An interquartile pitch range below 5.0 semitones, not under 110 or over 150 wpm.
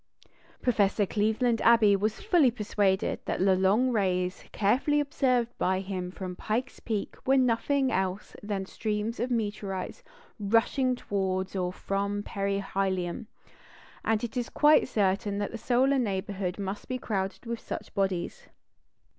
Yes: average, 3.9 semitones; average, 140 wpm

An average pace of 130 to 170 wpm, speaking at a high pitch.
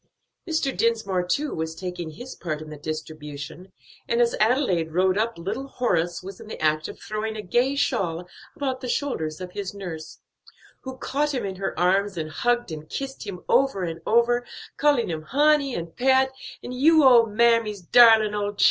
No: average, 185 wpm; high, 210 Hz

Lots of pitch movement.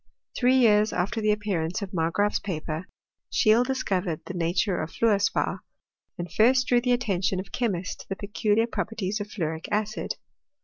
No: average, 3.8 semitones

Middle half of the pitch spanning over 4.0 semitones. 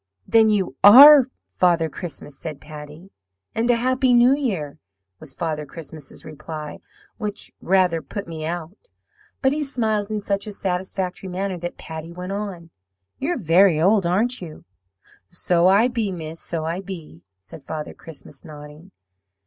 Yes: average, 4.8 semitones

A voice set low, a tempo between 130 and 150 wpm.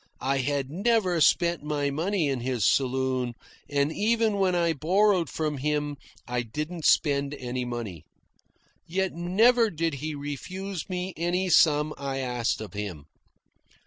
No: medium, 150 Hz; average, 145 wpm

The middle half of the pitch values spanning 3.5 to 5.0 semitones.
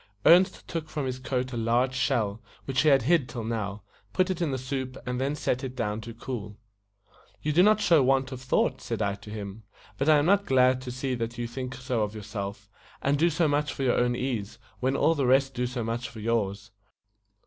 No: average, 3.1 semitones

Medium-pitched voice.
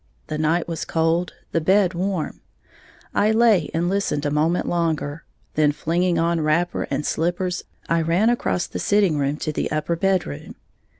Yes: medium, 170 Hz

